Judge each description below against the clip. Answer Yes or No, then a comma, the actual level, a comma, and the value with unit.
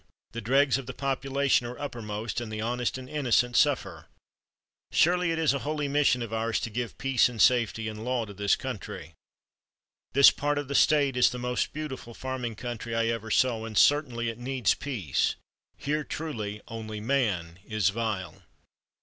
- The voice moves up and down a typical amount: Yes, average, 3.7 semitones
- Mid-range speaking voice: No, low, 120 Hz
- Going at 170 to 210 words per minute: Yes, average, 175 wpm